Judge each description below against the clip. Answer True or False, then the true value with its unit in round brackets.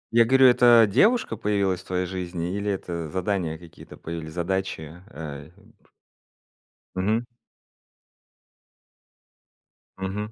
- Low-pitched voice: True (95 Hz)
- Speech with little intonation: False (3.6 semitones)